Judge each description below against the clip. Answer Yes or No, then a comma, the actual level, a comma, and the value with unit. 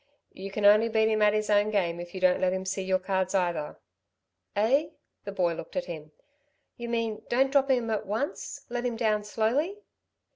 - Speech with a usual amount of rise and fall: Yes, average, 3.5 semitones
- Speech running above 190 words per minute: Yes, fast, 205 wpm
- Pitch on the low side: No, high, 210 Hz